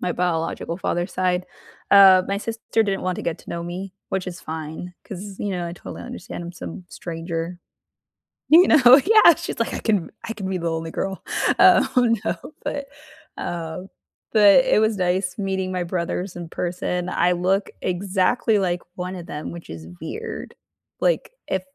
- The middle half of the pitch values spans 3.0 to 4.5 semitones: No, narrow, 2.5 semitones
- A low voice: No, medium, 185 Hz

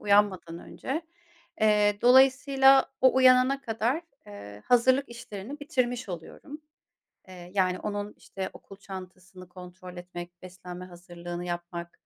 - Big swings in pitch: Yes, wide, 6.1 semitones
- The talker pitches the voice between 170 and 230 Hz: Yes, high, 195 Hz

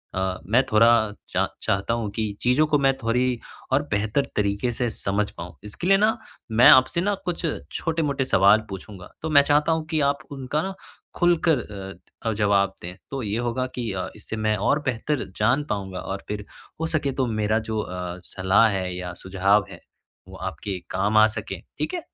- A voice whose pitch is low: Yes, low, 110 Hz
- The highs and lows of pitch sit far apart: Yes, wide, 5.9 semitones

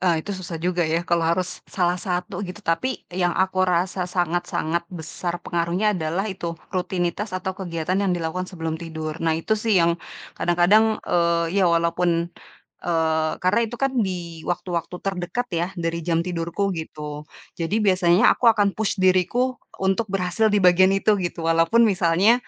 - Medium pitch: Yes, medium, 180 Hz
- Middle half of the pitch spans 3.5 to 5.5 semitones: No, narrow, 2.4 semitones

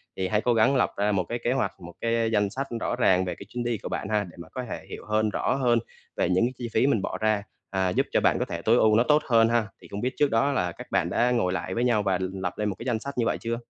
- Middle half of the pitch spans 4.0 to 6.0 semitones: No, average, 3.6 semitones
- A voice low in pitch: Yes, low, 110 Hz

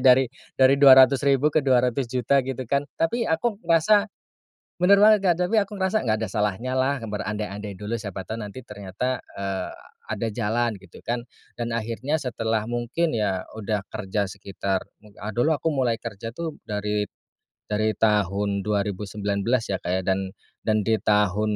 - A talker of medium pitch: No, low, 115 Hz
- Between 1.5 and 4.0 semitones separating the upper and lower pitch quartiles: No, average, 4.5 semitones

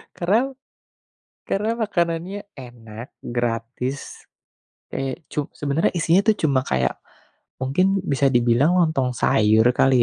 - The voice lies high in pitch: No, medium, 140 Hz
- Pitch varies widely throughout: Yes, wide, 6.8 semitones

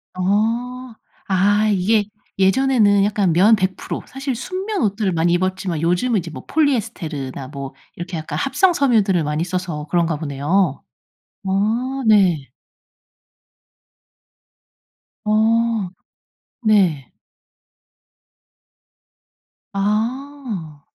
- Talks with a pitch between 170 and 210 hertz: Yes, high, 200 Hz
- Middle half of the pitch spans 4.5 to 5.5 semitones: Yes, average, 5.2 semitones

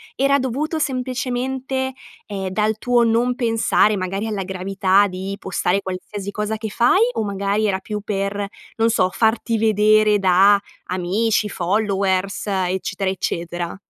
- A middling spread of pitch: Yes, average, 3.0 semitones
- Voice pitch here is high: Yes, high, 205 Hz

